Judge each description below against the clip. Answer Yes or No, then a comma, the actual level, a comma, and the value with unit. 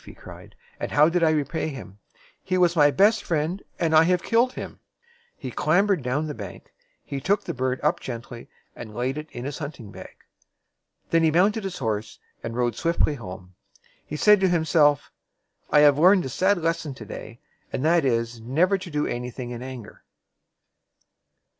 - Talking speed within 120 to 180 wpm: No, average, 190 wpm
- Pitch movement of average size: No, wide, 5.8 semitones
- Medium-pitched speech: Yes, medium, 150 Hz